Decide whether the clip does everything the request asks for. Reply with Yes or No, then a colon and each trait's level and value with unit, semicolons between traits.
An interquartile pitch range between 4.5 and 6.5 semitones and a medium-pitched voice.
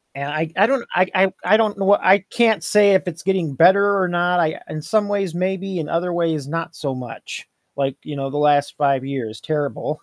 Yes: average, 4.8 semitones; medium, 170 Hz